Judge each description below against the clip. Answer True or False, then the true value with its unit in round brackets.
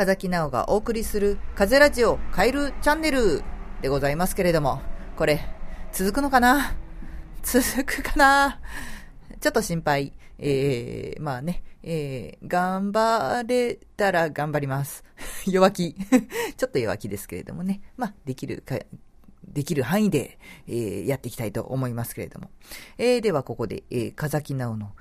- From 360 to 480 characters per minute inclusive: False (290 characters per minute)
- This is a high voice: False (170 Hz)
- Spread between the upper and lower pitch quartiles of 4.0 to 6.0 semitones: False (9.0 semitones)